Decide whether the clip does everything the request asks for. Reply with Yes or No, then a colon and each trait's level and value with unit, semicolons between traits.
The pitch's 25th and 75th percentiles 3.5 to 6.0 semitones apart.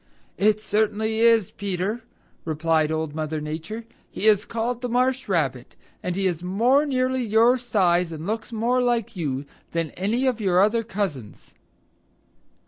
Yes: average, 5.3 semitones